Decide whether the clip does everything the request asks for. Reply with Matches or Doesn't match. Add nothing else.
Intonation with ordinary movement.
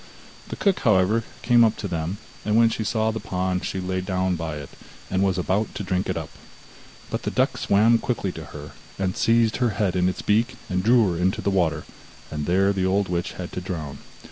Matches